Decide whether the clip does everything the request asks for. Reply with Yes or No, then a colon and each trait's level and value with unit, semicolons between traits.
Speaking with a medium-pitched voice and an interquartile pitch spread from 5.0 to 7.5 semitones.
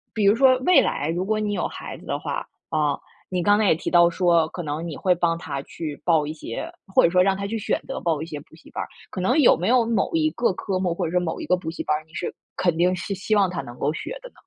No: medium, 180 Hz; average, 4.0 semitones